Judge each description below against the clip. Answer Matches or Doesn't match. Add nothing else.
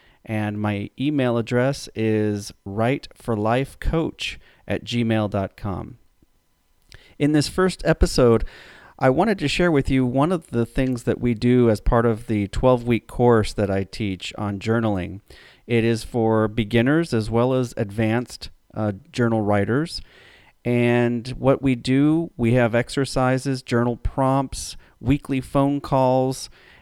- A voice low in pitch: Matches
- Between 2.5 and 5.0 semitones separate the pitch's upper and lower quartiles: Matches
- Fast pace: Doesn't match